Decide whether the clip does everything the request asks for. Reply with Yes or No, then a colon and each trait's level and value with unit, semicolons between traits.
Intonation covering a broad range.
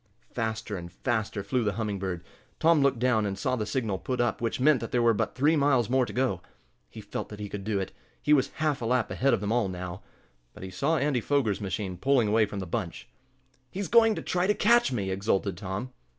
No: average, 4.9 semitones